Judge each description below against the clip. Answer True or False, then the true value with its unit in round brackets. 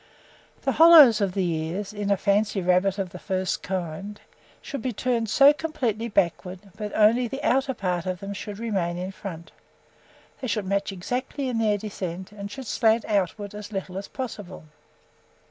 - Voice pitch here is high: True (205 Hz)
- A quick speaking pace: False (180 wpm)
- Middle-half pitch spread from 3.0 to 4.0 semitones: True (3.5 semitones)